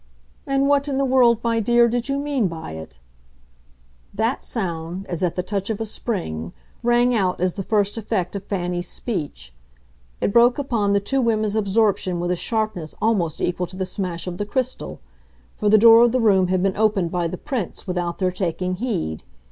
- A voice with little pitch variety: No, average, 4.6 semitones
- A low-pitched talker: No, high, 200 Hz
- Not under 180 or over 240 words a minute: Yes, average, 195 wpm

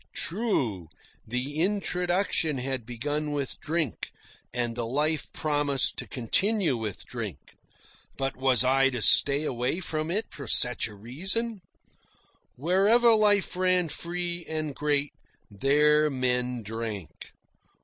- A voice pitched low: No, medium, 145 Hz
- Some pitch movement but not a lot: No, wide, 5.9 semitones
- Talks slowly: Yes, slow, 120 wpm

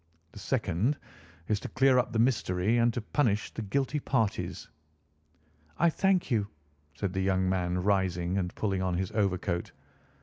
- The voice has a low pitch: Yes, low, 100 Hz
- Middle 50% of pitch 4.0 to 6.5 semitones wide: Yes, average, 4.6 semitones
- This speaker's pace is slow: No, average, 160 wpm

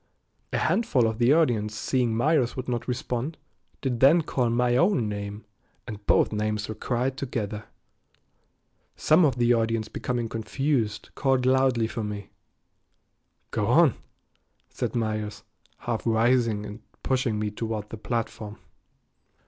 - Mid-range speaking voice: No, low, 115 Hz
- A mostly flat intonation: No, average, 3.1 semitones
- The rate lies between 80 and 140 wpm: Yes, slow, 135 wpm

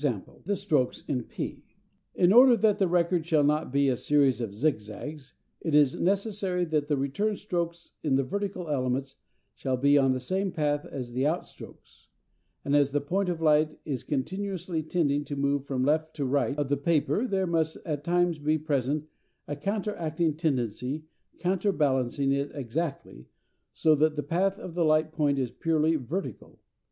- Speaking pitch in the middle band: Yes, medium, 150 Hz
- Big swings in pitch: No, average, 3.9 semitones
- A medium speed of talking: Yes, average, 175 wpm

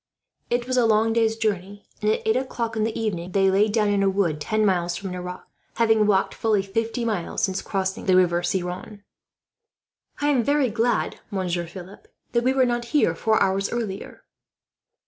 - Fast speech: No, average, 185 wpm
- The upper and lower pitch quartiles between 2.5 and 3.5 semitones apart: Yes, average, 3.2 semitones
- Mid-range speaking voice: No, high, 210 Hz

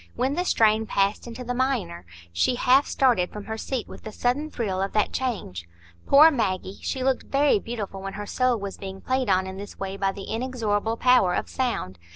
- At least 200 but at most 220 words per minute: Yes, fast, 205 wpm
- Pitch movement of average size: Yes, average, 4.7 semitones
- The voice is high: Yes, high, 220 Hz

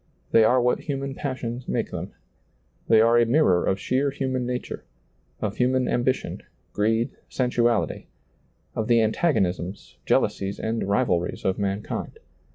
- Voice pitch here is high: No, low, 120 Hz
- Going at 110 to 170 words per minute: Yes, average, 140 wpm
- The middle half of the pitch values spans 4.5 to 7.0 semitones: No, average, 3.7 semitones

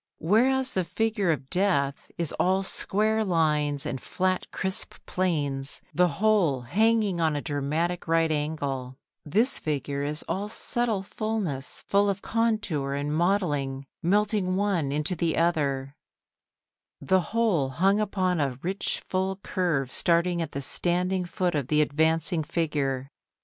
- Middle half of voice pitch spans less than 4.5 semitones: No, average, 5.1 semitones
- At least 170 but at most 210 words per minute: No, average, 140 wpm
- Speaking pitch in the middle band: Yes, medium, 170 Hz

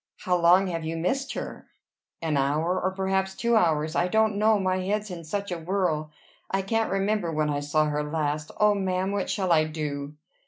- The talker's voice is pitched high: No, medium, 180 Hz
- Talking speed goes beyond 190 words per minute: Yes, average, 200 wpm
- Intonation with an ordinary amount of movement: Yes, average, 4.0 semitones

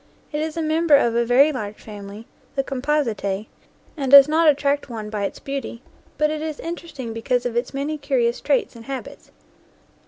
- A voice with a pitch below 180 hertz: No, very high, 270 Hz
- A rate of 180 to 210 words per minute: Yes, average, 185 wpm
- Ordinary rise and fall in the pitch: Yes, average, 4.5 semitones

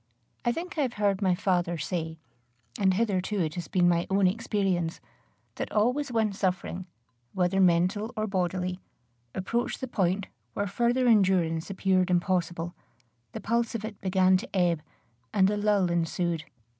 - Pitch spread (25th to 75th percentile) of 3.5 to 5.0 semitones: No, average, 3.0 semitones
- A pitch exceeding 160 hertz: Yes, high, 190 Hz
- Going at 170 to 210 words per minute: No, average, 155 wpm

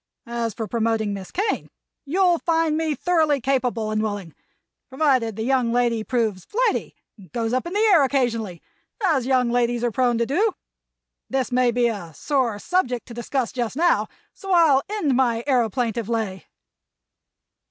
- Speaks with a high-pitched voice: Yes, high, 245 Hz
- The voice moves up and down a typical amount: Yes, average, 4.2 semitones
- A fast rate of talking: No, average, 160 wpm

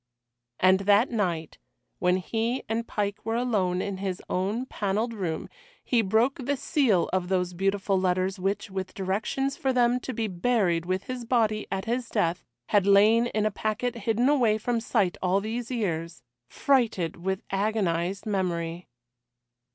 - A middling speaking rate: Yes, average, 160 wpm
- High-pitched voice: Yes, high, 205 Hz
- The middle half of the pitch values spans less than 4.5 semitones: Yes, average, 3.8 semitones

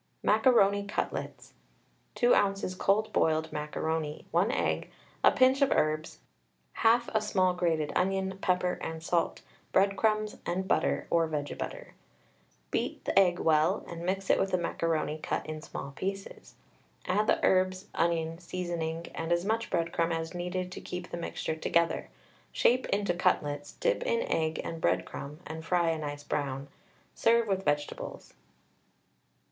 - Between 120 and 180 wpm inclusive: Yes, average, 150 wpm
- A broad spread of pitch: No, average, 3.5 semitones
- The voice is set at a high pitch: No, medium, 175 Hz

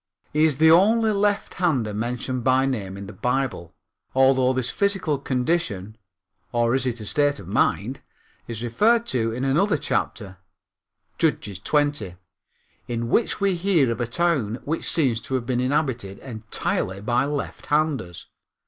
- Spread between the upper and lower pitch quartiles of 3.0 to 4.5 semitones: No, average, 5.2 semitones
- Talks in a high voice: No, low, 130 Hz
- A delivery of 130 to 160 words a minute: Yes, average, 150 wpm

